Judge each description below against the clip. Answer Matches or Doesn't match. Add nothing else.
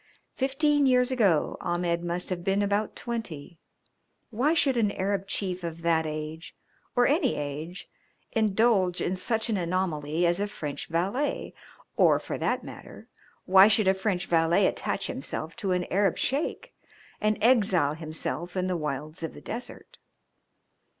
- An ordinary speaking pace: Matches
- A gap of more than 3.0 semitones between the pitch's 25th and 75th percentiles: Matches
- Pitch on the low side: Doesn't match